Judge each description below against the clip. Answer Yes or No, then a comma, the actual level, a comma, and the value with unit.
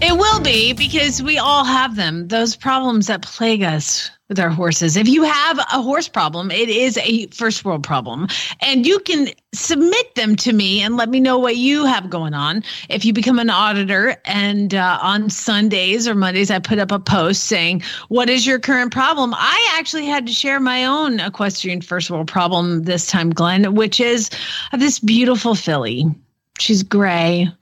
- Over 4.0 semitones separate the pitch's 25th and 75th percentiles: Yes, average, 5.3 semitones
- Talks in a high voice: Yes, high, 220 Hz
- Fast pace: No, average, 190 wpm